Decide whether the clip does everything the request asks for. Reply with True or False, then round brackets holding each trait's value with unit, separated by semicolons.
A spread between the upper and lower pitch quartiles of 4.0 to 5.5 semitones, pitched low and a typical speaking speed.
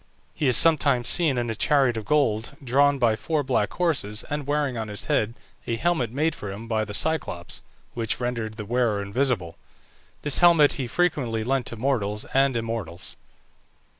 True (4.6 semitones; 120 Hz; 175 wpm)